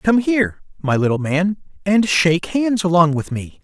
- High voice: No, medium, 180 Hz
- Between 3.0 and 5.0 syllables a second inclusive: Yes, 4.7 syllables/s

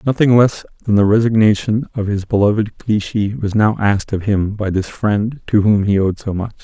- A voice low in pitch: Yes, low, 105 Hz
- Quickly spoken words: Yes, fast, 210 wpm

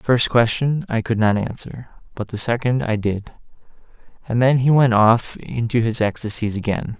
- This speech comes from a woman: No, male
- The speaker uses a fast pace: No, average, 180 wpm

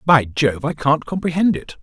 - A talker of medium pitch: Yes, medium, 150 Hz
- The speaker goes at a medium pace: Yes, average, 195 wpm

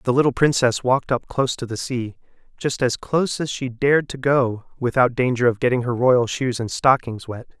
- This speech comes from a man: Yes, male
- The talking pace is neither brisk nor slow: No, fast, 215 wpm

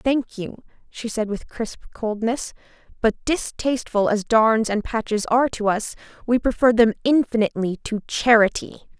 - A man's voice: No, female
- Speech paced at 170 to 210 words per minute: No, average, 140 wpm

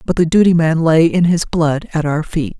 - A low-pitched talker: No, medium, 165 Hz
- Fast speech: Yes, fast, 255 wpm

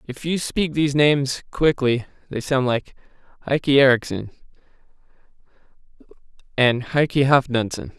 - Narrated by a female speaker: No, male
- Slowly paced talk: Yes, slow, 105 wpm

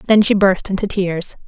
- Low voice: No, high, 190 Hz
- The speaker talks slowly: No, fast, 205 wpm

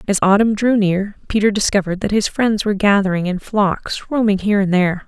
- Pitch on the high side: Yes, high, 200 Hz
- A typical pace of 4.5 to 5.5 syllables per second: No, 5.9 syllables/s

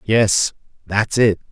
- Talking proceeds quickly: No, slow, 120 wpm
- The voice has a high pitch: No, low, 105 Hz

